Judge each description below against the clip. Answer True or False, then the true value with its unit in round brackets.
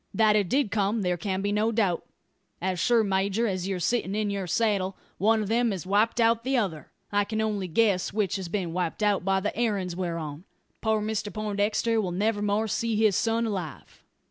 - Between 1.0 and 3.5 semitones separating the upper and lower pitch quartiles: True (2.7 semitones)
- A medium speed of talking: False (210 wpm)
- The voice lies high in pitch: True (205 Hz)